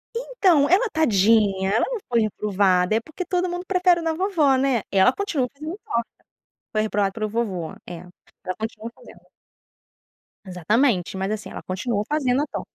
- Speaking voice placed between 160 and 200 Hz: No, high, 235 Hz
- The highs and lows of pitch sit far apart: Yes, wide, 7.9 semitones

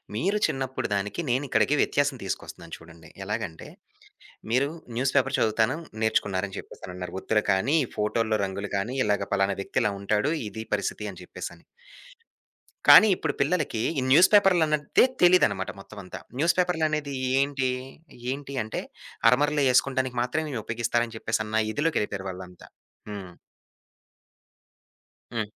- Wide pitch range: Yes, wide, 5.9 semitones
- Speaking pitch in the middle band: No, low, 115 Hz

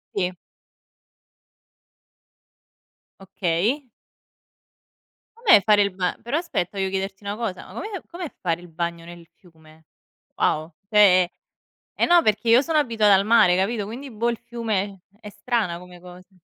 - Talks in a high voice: Yes, high, 200 Hz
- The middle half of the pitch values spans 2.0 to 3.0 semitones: No, average, 4.5 semitones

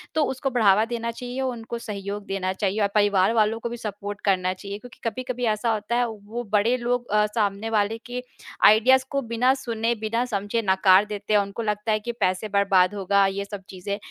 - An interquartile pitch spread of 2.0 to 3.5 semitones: Yes, average, 2.9 semitones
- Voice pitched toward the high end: Yes, high, 215 Hz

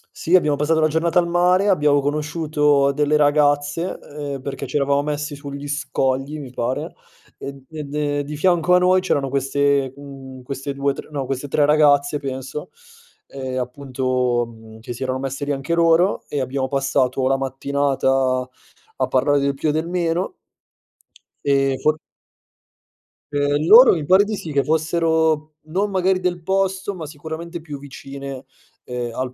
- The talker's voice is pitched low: No, medium, 145 Hz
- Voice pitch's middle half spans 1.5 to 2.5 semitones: No, average, 2.9 semitones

